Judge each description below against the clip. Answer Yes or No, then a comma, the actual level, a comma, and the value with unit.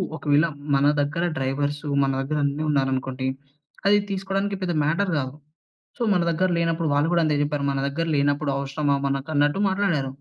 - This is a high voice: No, medium, 145 Hz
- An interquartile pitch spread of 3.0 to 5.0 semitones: Yes, average, 3.3 semitones